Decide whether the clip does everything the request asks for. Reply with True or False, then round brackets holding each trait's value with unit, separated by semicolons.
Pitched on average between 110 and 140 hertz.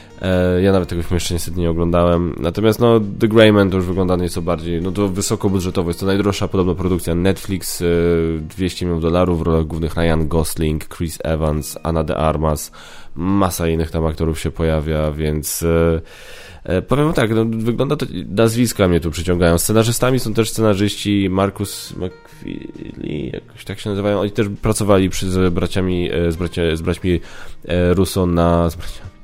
False (90 Hz)